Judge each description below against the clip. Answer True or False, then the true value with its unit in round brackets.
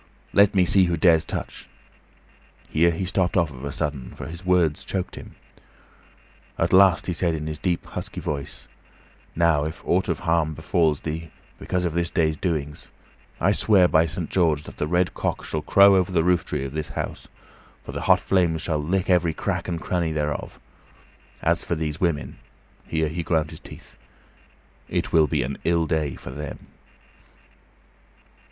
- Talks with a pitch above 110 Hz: False (80 Hz)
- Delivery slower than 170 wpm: False (175 wpm)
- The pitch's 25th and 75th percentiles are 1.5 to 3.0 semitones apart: True (2.7 semitones)